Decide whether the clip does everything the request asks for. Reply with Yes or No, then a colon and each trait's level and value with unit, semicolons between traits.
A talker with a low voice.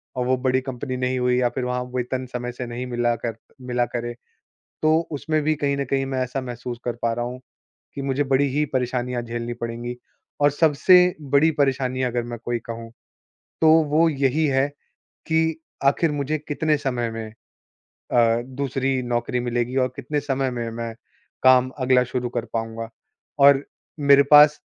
Yes: low, 130 Hz